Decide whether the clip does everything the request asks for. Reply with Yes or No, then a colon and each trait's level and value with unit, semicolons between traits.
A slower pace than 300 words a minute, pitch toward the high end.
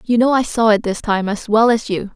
No: fast, 305 wpm; high, 220 Hz